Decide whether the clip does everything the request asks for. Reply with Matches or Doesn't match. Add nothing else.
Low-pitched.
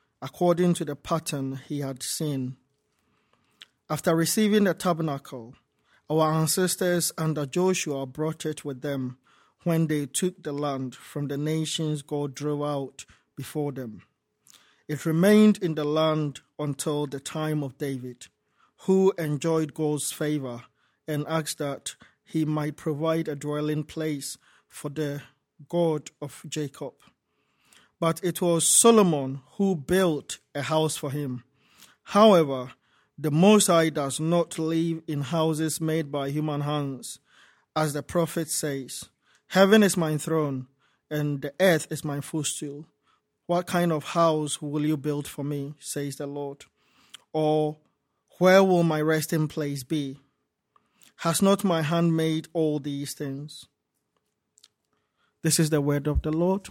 Doesn't match